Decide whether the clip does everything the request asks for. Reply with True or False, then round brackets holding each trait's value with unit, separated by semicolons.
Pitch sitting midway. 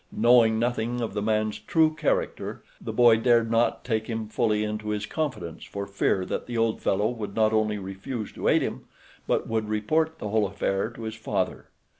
False (110 Hz)